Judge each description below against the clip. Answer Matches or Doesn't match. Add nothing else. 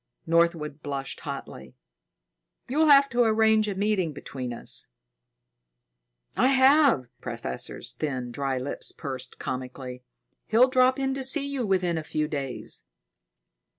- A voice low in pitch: Doesn't match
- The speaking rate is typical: Doesn't match